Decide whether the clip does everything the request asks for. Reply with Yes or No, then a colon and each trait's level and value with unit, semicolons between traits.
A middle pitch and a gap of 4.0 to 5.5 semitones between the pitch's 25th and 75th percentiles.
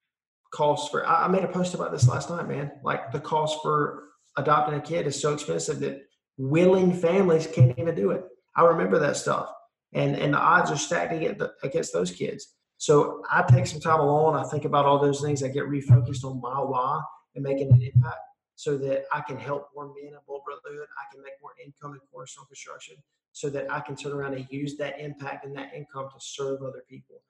No: medium, 145 Hz; narrow, 2.5 semitones